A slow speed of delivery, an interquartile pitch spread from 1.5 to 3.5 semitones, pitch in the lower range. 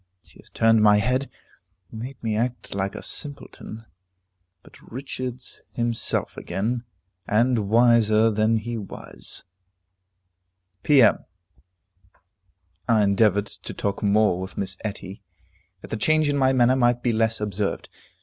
Yes: slow, 130 wpm; average, 2.9 semitones; low, 115 Hz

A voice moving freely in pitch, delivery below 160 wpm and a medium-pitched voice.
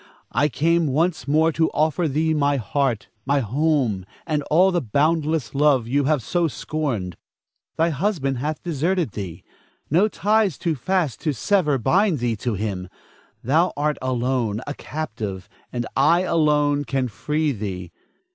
No: average, 4.8 semitones; average, 150 wpm; medium, 145 Hz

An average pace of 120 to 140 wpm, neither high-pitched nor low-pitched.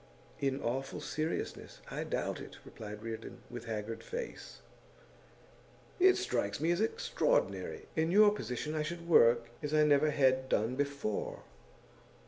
Yes: slow, 135 wpm; medium, 145 Hz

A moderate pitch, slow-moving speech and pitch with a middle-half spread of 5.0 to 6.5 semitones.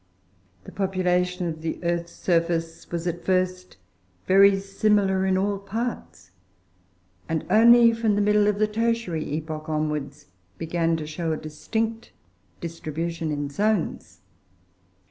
No: medium, 180 Hz; slow, 125 wpm; average, 4.0 semitones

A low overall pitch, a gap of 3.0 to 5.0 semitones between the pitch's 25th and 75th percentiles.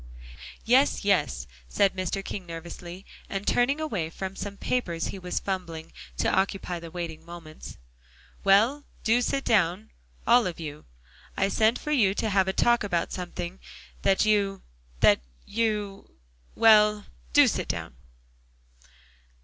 No: high, 195 Hz; average, 3.9 semitones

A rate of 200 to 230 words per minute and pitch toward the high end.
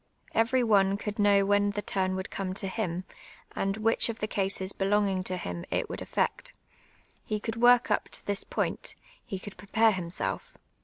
No: average, 190 wpm; high, 200 Hz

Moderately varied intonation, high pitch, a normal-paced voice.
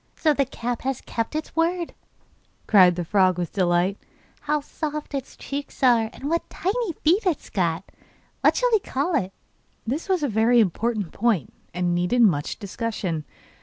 No: wide, 8.4 semitones; high, 235 Hz; average, 170 wpm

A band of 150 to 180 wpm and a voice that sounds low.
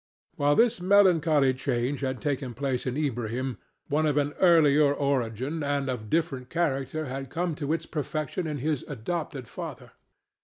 No: average, 155 wpm; medium, 145 Hz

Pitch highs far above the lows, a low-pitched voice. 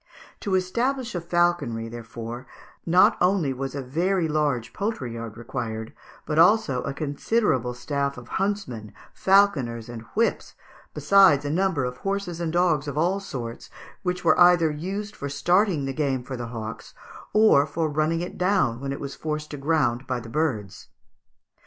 No: wide, 6.3 semitones; medium, 150 Hz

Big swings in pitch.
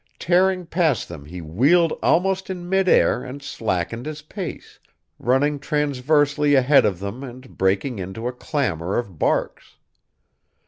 Yes: wide, 7.0 semitones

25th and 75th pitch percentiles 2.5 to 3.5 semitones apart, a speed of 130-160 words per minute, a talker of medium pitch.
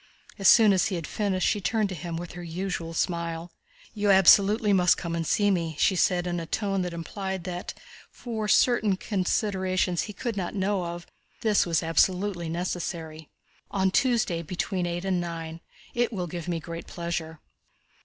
No: average, 2.8 semitones; average, 175 wpm; medium, 180 Hz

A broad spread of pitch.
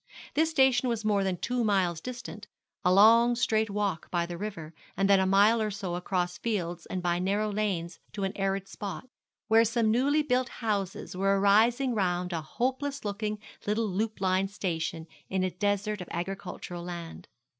No: average, 3.6 semitones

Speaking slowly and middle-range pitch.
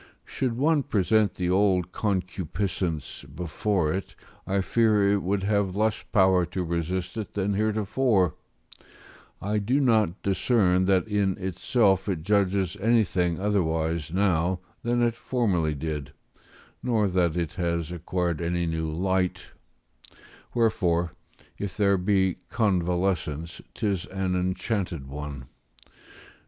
No: slow, 120 wpm; very low, 95 Hz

